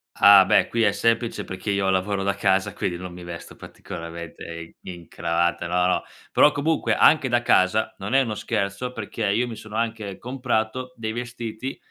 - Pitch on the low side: Yes, low, 105 Hz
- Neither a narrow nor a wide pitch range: Yes, average, 4.0 semitones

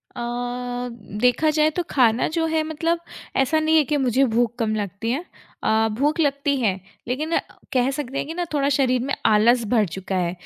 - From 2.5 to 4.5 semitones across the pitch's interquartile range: No, average, 5.1 semitones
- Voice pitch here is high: Yes, very high, 260 Hz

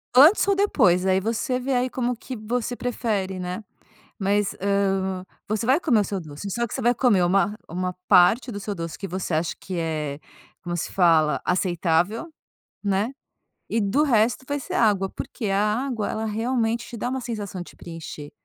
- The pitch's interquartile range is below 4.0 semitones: No, average, 4.8 semitones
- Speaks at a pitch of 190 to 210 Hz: Yes, high, 205 Hz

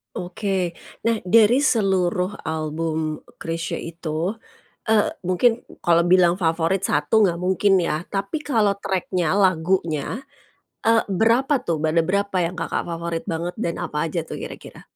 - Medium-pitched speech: Yes, medium, 180 Hz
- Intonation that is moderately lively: Yes, average, 3.5 semitones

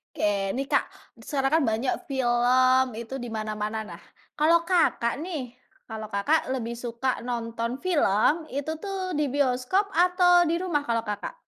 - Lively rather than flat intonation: Yes, wide, 5.7 semitones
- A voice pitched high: Yes, very high, 255 Hz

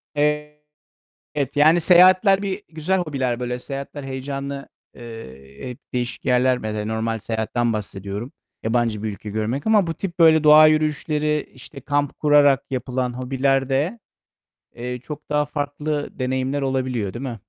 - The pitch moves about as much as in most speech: Yes, average, 3.8 semitones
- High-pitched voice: No, low, 135 Hz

